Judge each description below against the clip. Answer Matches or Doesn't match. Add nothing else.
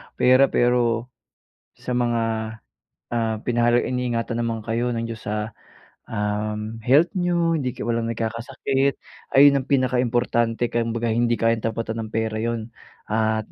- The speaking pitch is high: Doesn't match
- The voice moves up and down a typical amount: Doesn't match